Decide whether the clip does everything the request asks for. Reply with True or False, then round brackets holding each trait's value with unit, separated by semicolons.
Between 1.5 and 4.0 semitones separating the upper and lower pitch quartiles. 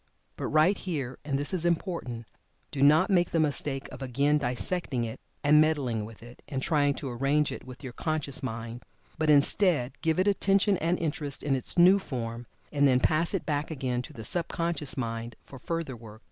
False (4.6 semitones)